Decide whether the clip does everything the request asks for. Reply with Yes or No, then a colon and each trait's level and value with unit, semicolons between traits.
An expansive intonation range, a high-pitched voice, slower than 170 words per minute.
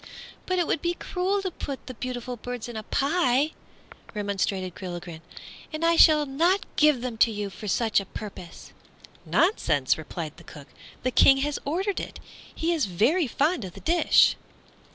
No: wide, 8.3 semitones; very high, 255 Hz; average, 175 wpm